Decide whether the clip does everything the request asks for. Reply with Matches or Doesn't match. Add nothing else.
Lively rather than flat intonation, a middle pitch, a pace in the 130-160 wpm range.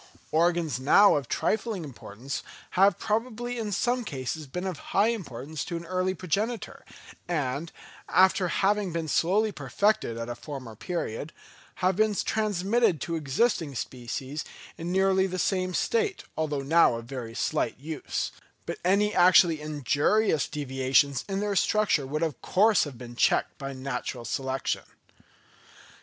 Matches